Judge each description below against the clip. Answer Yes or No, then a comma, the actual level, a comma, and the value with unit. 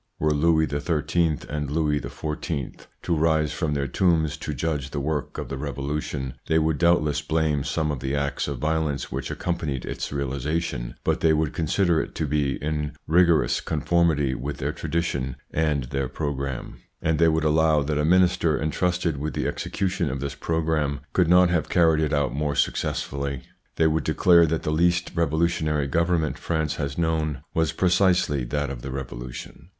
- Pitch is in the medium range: No, very low, 75 Hz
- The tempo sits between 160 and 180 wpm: Yes, average, 175 wpm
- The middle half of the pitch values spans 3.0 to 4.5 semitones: No, narrow, 2.5 semitones